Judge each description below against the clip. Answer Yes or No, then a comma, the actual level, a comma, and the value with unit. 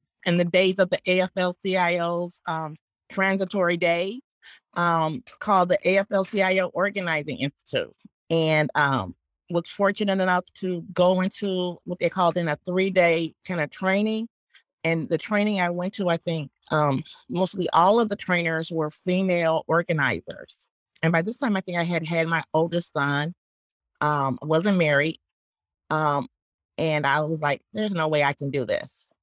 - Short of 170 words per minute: Yes, average, 155 wpm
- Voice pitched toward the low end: No, medium, 175 Hz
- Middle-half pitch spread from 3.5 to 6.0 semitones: No, average, 3.1 semitones